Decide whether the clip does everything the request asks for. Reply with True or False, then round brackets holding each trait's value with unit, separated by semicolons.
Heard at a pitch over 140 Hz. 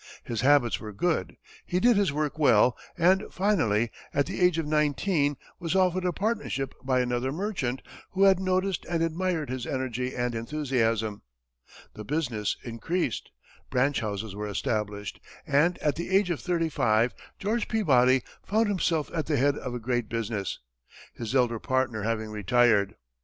False (135 Hz)